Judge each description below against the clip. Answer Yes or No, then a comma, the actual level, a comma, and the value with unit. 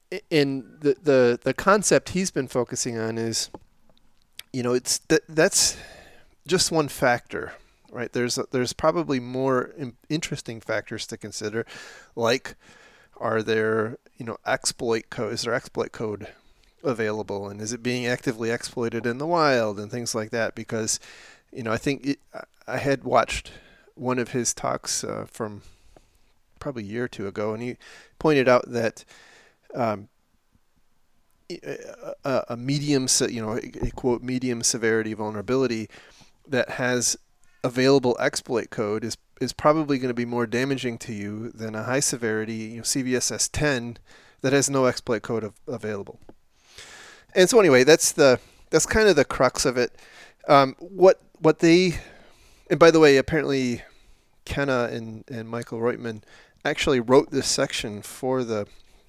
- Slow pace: No, average, 155 wpm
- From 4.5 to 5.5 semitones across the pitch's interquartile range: No, average, 3.6 semitones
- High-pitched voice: No, low, 125 Hz